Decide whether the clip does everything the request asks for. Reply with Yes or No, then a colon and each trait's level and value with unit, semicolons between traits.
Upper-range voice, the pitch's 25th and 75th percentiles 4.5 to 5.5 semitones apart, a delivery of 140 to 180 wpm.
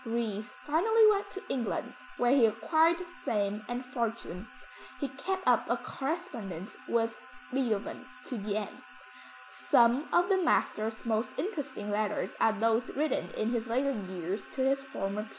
Yes: high, 235 Hz; average, 4.9 semitones; average, 150 wpm